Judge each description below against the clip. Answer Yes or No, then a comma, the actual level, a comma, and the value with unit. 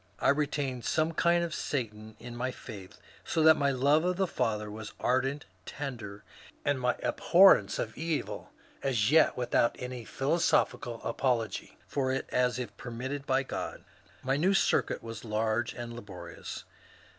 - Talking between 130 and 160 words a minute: Yes, average, 155 wpm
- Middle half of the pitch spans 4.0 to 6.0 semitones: Yes, average, 4.3 semitones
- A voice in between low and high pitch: No, low, 125 Hz